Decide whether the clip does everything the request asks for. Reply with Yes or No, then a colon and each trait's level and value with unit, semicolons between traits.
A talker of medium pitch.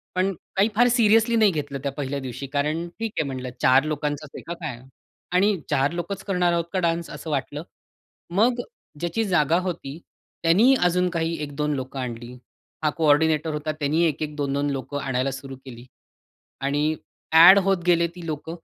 Yes: medium, 155 Hz